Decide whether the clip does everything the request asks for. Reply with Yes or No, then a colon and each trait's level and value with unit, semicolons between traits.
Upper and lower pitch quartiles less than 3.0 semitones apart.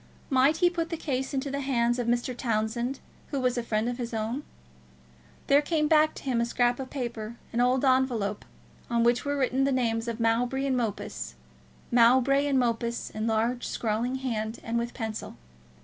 Yes: narrow, 2.4 semitones